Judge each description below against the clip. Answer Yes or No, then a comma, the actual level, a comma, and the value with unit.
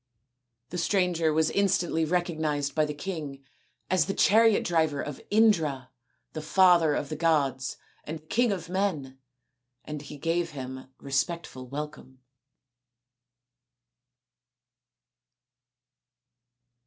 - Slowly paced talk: Yes, slow, 105 wpm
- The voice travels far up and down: No, average, 3.6 semitones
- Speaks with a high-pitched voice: No, medium, 155 Hz